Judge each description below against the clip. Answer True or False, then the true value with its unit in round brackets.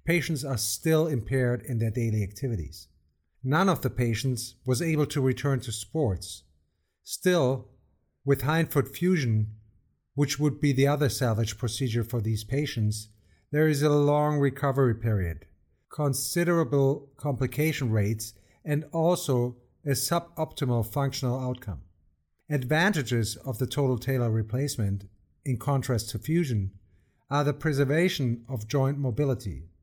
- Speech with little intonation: False (5.2 semitones)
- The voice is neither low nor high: False (130 Hz)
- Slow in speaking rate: True (125 wpm)